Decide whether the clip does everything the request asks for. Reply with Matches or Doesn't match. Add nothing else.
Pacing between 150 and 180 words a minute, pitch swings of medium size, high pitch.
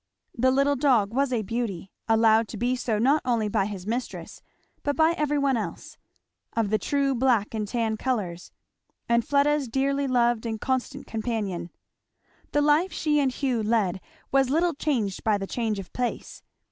Matches